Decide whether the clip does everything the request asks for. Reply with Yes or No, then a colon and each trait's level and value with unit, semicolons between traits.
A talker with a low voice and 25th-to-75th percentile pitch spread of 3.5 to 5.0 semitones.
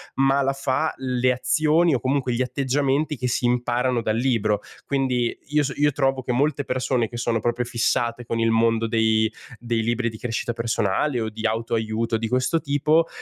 No: low, 125 Hz; average, 2.9 semitones